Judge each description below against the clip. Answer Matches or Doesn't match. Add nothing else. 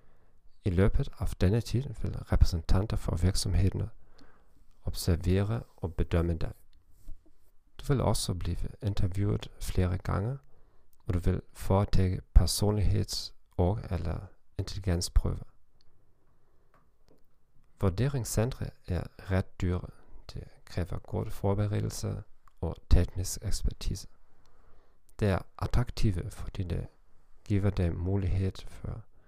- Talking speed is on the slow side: Matches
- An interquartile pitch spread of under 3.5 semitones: Matches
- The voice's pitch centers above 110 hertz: Doesn't match